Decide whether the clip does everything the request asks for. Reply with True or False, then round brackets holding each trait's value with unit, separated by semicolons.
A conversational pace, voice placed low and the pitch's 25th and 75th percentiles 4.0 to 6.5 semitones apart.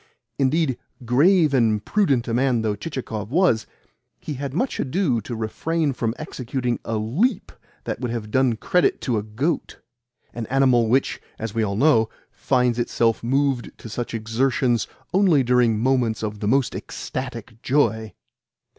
False (155 wpm; 125 Hz; 3.5 semitones)